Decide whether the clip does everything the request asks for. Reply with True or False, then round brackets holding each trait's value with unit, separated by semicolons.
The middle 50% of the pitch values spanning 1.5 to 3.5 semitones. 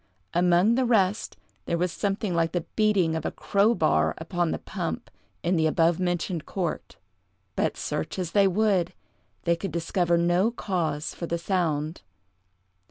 True (2.8 semitones)